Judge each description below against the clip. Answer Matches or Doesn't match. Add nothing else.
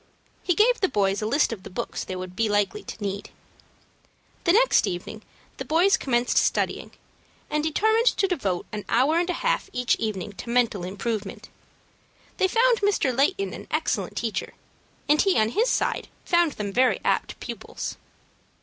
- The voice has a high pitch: Matches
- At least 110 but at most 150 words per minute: Doesn't match